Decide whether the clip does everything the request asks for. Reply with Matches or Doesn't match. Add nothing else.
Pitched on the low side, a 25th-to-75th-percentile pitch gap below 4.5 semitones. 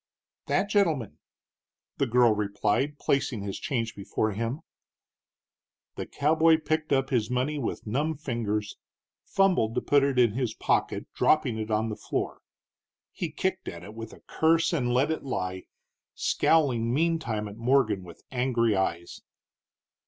Doesn't match